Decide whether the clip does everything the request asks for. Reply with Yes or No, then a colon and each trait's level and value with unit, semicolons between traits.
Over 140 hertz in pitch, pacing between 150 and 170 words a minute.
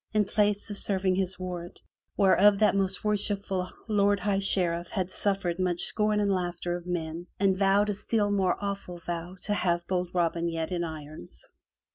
No: high, 190 Hz; average, 180 wpm